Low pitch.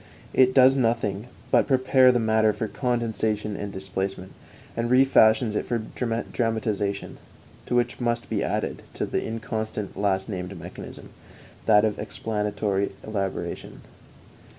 Yes: low, 110 Hz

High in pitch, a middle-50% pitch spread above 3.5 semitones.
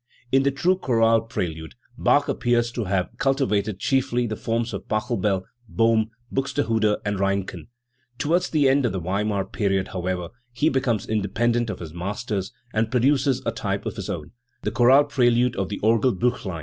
No: low, 115 Hz; average, 4.2 semitones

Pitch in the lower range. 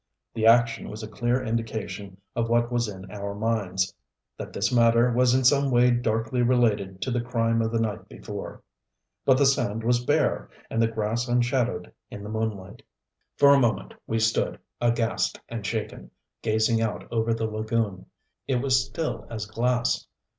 Yes: low, 115 Hz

